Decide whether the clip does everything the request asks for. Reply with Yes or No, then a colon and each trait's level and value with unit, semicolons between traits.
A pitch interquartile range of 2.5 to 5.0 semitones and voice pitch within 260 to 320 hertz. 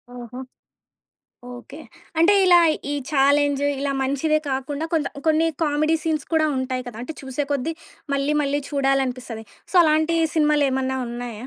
Yes: average, 2.9 semitones; very high, 280 Hz